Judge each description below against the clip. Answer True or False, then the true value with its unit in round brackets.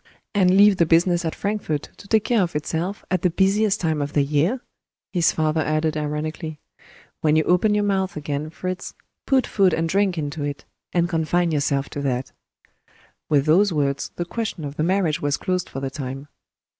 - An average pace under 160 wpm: False (190 wpm)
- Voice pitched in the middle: True (165 Hz)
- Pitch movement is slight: False (4.1 semitones)